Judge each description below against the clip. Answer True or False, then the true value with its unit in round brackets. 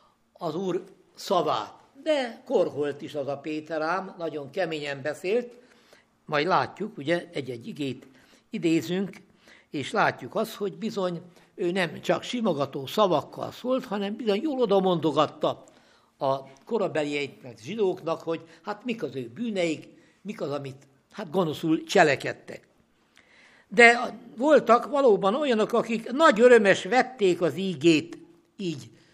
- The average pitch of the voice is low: False (185 Hz)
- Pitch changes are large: True (6.3 semitones)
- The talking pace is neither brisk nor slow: True (120 wpm)